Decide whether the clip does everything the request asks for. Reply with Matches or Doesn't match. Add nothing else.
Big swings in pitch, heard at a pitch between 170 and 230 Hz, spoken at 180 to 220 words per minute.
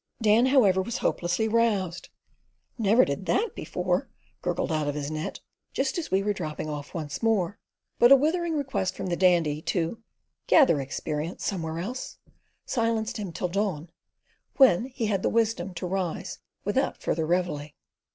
Doesn't match